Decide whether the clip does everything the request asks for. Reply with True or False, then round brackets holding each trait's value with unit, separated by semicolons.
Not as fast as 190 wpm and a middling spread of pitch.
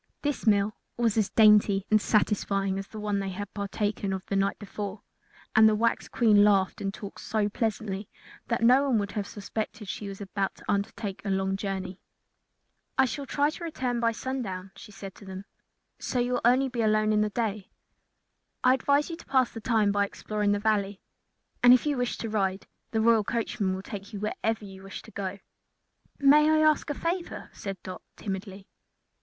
False (195 wpm; 3.0 semitones)